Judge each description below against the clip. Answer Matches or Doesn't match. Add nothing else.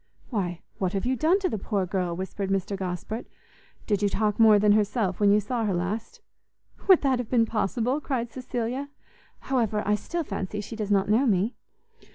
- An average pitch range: Matches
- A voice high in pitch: Matches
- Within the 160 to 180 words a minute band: Doesn't match